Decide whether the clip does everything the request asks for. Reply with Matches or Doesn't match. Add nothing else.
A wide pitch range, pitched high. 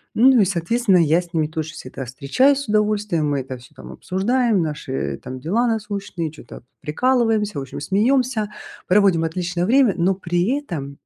Doesn't match